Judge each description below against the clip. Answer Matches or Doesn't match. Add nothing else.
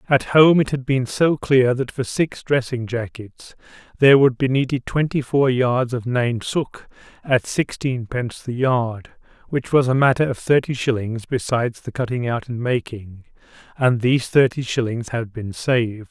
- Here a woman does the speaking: Doesn't match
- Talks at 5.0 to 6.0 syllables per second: Doesn't match